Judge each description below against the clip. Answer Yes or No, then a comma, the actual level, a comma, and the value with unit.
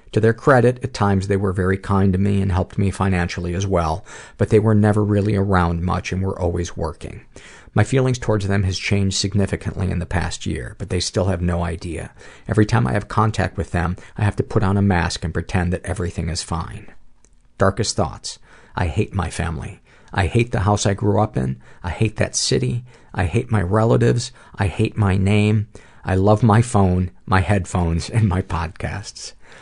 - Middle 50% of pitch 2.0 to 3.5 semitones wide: Yes, average, 3.0 semitones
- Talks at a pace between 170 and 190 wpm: No, fast, 205 wpm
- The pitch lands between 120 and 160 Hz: No, low, 100 Hz